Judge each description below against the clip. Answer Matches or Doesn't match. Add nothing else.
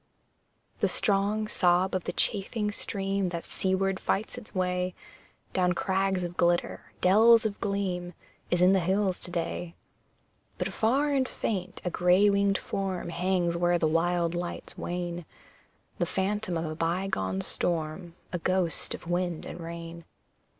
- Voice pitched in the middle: Matches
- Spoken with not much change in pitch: Matches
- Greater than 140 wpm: Matches